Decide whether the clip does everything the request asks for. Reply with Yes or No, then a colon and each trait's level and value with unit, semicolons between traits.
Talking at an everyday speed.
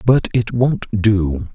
Yes: average, 155 wpm